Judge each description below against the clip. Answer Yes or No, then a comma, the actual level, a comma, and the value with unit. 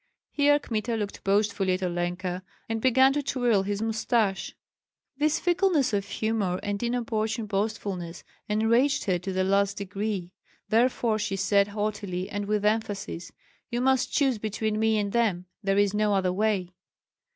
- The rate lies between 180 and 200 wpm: No, average, 150 wpm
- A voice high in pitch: Yes, high, 210 Hz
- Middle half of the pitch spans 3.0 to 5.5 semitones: No, narrow, 2.6 semitones